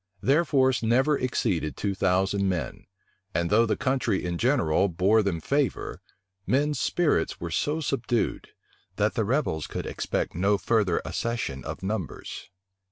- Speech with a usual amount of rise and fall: No, wide, 6.2 semitones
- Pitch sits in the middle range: No, low, 110 Hz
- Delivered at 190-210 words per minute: No, average, 145 wpm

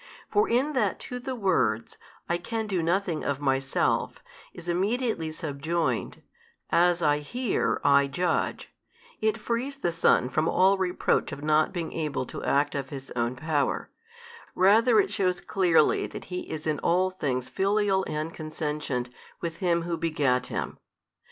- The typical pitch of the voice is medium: Yes, medium, 170 Hz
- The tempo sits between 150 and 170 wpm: Yes, average, 155 wpm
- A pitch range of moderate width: Yes, average, 4.9 semitones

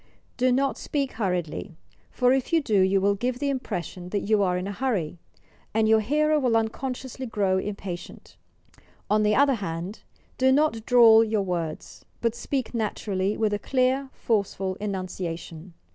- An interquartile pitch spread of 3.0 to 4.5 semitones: No, average, 5.1 semitones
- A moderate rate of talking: Yes, average, 160 wpm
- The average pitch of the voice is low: No, high, 215 Hz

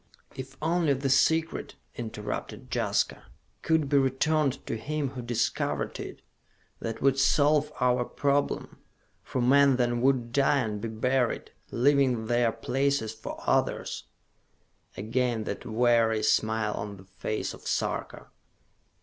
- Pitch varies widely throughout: No, average, 3.6 semitones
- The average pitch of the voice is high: No, low, 125 Hz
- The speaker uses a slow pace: Yes, slow, 130 wpm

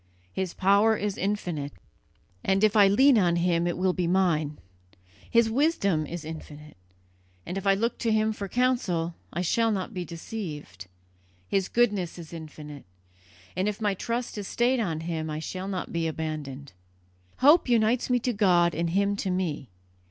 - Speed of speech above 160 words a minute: Yes, average, 170 wpm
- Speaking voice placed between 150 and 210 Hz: Yes, medium, 185 Hz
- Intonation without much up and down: No, average, 4.8 semitones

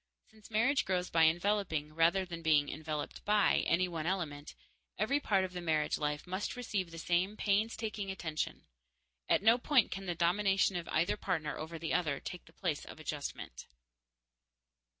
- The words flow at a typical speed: Yes, average, 170 wpm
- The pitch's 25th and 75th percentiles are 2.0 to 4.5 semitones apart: Yes, average, 4.0 semitones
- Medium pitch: Yes, medium, 175 Hz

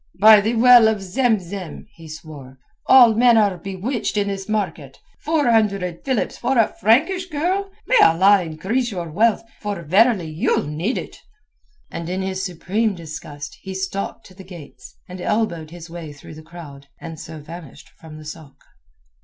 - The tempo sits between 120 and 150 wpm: No, average, 170 wpm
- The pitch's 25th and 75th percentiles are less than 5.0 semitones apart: No, wide, 5.5 semitones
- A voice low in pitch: No, high, 190 Hz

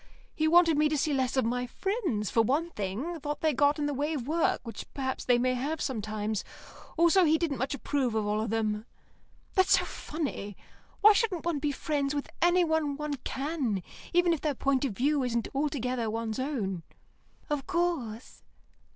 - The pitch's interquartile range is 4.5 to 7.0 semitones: Yes, average, 4.9 semitones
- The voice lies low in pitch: No, very high, 280 Hz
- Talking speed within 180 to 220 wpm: Yes, average, 185 wpm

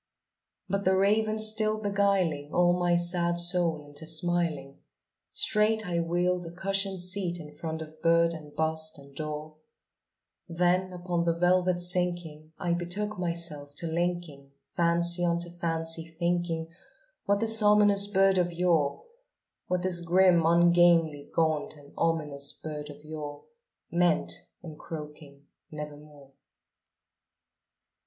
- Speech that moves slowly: Yes, slow, 130 wpm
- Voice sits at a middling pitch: Yes, medium, 170 Hz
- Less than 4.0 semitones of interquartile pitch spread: Yes, narrow, 2.4 semitones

